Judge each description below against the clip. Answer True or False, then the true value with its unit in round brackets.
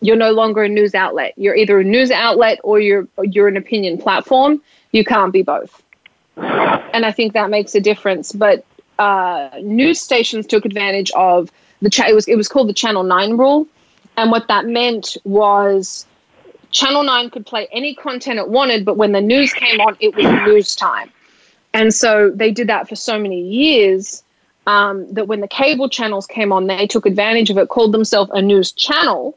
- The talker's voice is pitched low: False (220 Hz)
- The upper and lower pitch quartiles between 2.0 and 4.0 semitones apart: True (3.4 semitones)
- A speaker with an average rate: True (195 wpm)